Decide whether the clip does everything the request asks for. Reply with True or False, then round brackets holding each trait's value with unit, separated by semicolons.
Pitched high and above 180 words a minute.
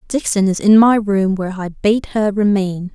True (200 Hz; 205 wpm)